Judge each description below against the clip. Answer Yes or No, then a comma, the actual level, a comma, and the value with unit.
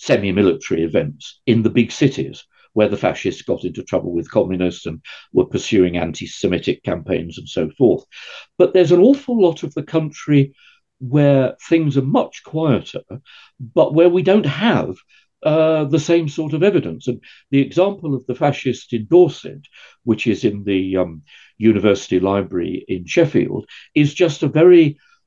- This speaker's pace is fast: No, average, 165 wpm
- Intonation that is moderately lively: No, wide, 6.9 semitones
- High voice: No, medium, 145 Hz